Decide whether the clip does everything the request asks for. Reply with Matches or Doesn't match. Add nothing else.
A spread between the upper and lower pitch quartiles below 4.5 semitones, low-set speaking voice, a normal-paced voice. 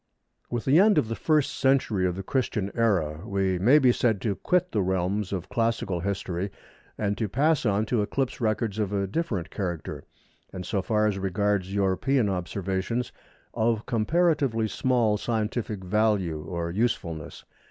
Matches